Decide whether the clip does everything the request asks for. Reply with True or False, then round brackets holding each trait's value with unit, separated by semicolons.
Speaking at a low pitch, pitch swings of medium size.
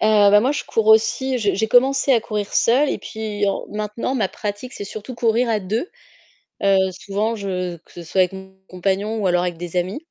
False (210 Hz; 3.2 semitones)